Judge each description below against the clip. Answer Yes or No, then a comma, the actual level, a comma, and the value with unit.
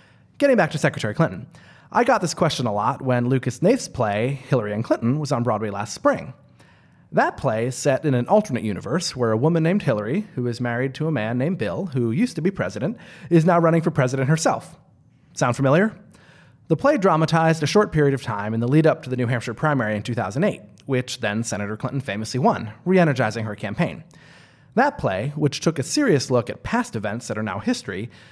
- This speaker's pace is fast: Yes, fast, 210 wpm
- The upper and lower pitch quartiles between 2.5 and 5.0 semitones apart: No, wide, 5.6 semitones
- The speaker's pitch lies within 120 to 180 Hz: Yes, low, 135 Hz